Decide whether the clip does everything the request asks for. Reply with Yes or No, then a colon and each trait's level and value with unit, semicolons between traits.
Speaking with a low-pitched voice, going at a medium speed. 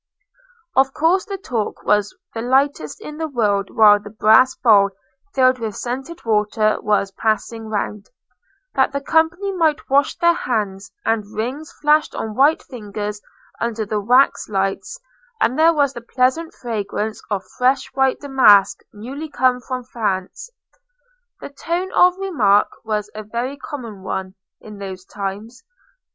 No: high, 235 Hz; average, 145 wpm